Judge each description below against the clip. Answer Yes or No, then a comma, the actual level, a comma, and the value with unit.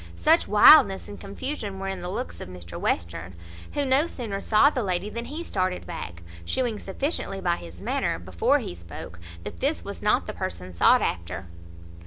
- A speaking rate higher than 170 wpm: Yes, average, 185 wpm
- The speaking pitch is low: No, high, 190 Hz